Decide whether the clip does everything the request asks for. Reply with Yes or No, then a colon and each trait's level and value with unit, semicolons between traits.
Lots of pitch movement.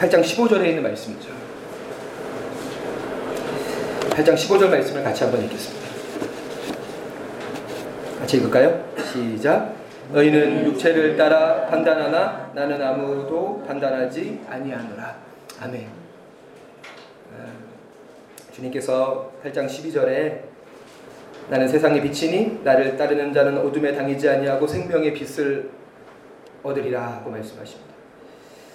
No: narrow, 2.5 semitones